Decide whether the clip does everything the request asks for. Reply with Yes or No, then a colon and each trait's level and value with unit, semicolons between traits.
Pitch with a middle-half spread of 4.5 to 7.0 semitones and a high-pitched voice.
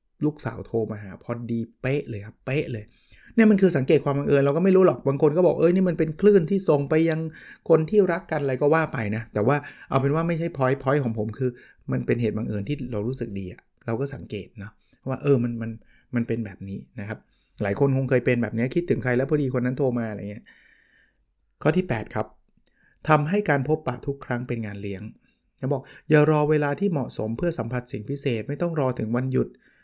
No: average, 5.1 semitones; low, 130 Hz